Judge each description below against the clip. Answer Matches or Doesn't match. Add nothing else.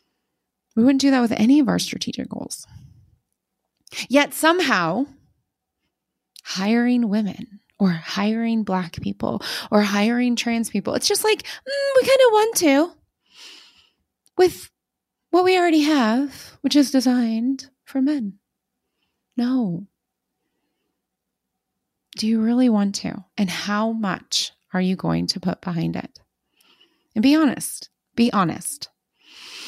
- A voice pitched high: Matches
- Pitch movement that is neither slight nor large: Doesn't match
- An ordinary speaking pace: Doesn't match